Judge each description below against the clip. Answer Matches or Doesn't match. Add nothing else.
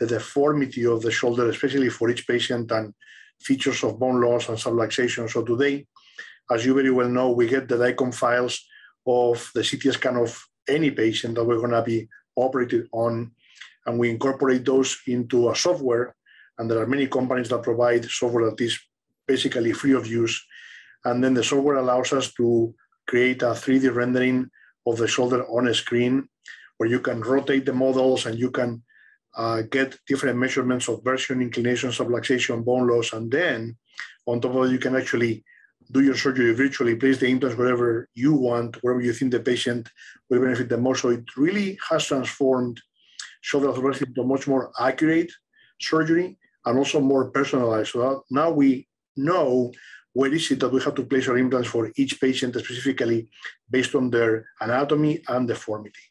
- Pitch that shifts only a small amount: Matches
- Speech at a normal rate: Matches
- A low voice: Matches